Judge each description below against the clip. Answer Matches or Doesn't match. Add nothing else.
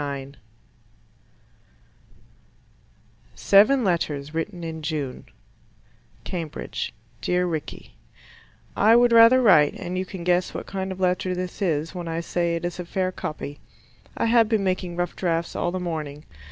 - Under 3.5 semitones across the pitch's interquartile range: Matches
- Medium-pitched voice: Matches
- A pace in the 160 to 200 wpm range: Doesn't match